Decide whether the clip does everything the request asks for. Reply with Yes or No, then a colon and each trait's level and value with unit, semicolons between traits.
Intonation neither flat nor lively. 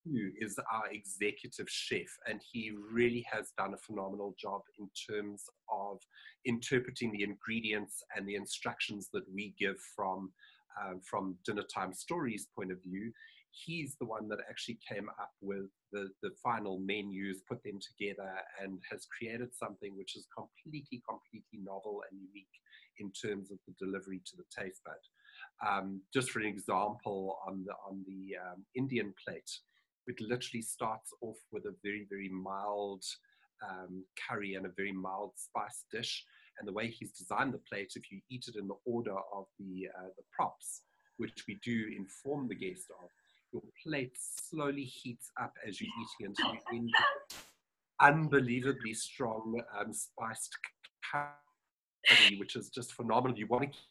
Yes: average, 3.7 semitones